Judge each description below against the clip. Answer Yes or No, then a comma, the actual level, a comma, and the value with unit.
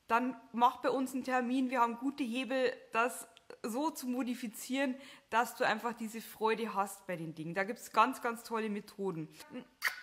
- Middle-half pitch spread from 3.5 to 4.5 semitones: No, narrow, 2.6 semitones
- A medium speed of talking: Yes, average, 180 wpm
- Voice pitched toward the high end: Yes, high, 235 Hz